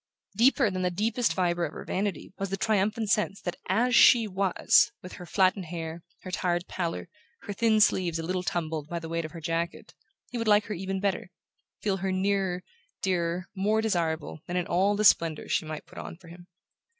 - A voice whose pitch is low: No, medium, 185 Hz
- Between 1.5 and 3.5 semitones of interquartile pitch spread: Yes, average, 3.0 semitones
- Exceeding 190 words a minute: Yes, fast, 205 wpm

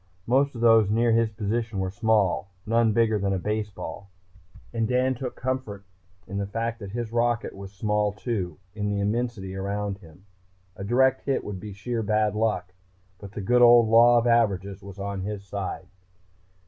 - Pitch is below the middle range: Yes, low, 105 Hz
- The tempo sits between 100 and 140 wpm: No, average, 180 wpm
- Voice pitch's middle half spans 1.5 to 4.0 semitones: Yes, average, 2.9 semitones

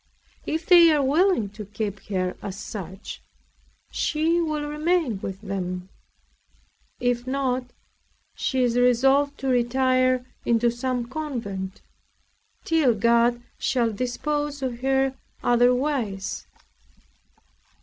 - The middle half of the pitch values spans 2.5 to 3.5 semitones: No, average, 4.4 semitones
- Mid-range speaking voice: No, very high, 250 Hz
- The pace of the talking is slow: Yes, slow, 105 wpm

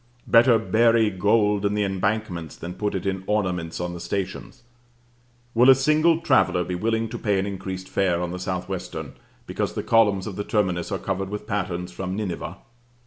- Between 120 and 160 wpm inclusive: No, average, 190 wpm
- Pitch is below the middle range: Yes, low, 100 Hz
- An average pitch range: Yes, average, 3.2 semitones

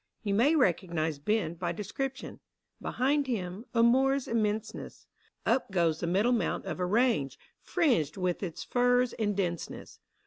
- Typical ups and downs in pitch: No, wide, 5.9 semitones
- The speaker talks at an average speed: Yes, average, 150 wpm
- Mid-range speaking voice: No, high, 210 Hz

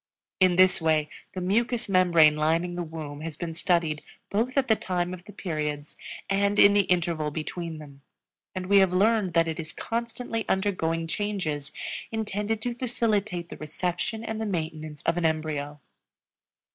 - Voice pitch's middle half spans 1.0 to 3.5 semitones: No, average, 4.5 semitones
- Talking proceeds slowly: No, average, 165 wpm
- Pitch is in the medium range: Yes, medium, 180 Hz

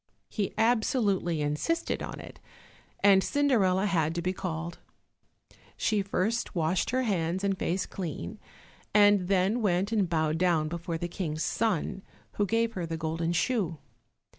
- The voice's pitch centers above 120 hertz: Yes, medium, 185 Hz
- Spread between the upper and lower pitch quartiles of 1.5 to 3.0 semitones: No, average, 4.0 semitones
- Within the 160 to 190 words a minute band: No, average, 145 wpm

